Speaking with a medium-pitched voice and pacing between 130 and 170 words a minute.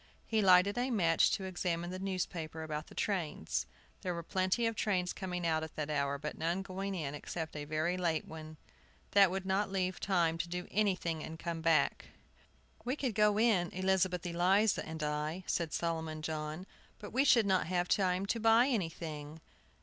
No: medium, 180 Hz; average, 185 wpm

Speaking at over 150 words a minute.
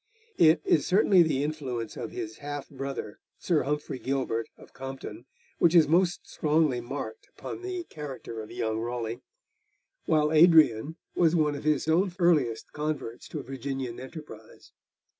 No: average, 145 wpm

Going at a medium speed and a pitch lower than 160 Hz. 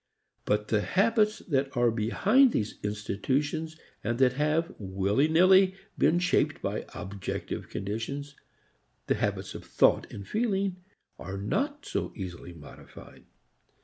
No: slow, 125 wpm; medium, 140 Hz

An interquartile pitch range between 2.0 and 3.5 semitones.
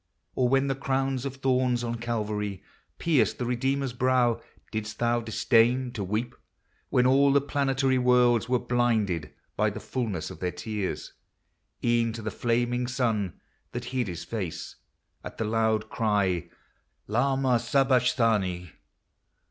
Yes: average, 3.0 semitones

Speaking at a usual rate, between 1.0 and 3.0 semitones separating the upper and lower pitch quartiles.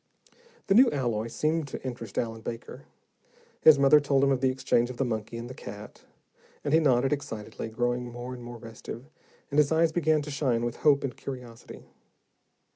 No: average, 190 wpm; average, 3.4 semitones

